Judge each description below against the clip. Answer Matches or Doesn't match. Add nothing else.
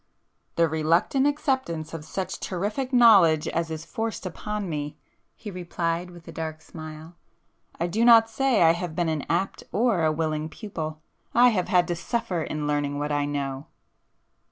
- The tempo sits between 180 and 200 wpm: Doesn't match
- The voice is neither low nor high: Matches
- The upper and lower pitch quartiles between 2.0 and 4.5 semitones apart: Doesn't match